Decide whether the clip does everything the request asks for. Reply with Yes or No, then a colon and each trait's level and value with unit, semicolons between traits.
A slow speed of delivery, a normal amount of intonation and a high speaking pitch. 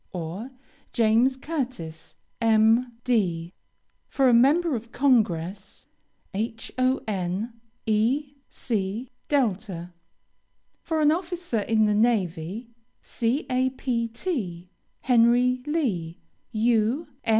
Yes: slow, 80 wpm; average, 4.2 semitones; high, 230 Hz